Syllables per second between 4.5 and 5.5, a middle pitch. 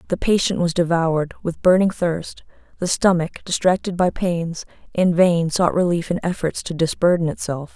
Yes: 5.0 syllables/s; medium, 175 Hz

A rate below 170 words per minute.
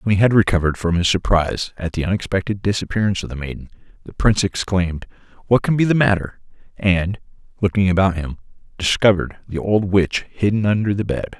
No: average, 180 wpm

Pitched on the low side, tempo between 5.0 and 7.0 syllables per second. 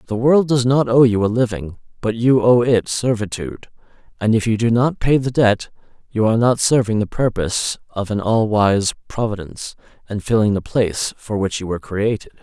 Yes: low, 110 Hz; 5.4 syllables/s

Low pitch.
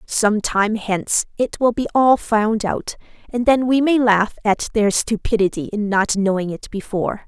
No: high, 215 Hz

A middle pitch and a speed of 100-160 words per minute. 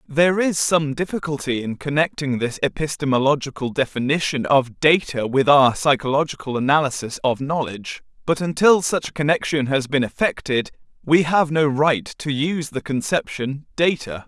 Yes: medium, 145 Hz; average, 145 wpm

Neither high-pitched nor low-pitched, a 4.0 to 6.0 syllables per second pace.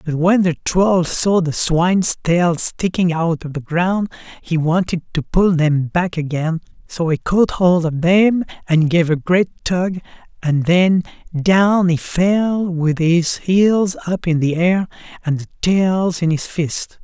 No: medium, 175 Hz; 3.6 syllables/s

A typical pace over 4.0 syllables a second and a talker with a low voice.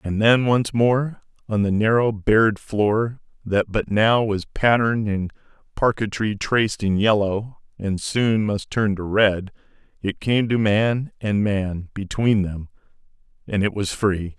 No: 3.9 syllables/s; low, 105 Hz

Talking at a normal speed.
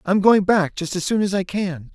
No: fast, 280 wpm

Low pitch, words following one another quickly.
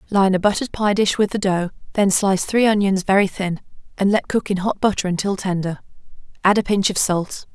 No: high, 195 Hz; fast, 215 wpm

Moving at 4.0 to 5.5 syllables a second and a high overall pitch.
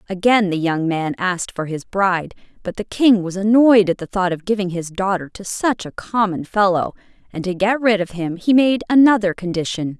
Yes: 5.2 syllables/s; high, 195 Hz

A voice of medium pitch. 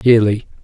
No: low, 110 Hz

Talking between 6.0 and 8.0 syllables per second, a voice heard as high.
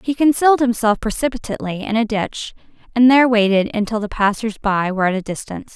Yes: 6.3 syllables/s; high, 225 Hz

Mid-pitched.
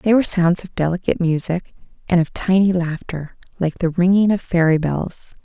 Yes: medium, 175 Hz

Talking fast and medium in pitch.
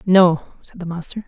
No: average, 190 wpm; medium, 180 Hz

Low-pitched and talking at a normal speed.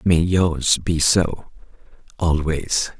No: very low, 85 Hz; slow, 100 wpm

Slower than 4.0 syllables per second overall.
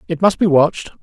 No: 6.5 syllables/s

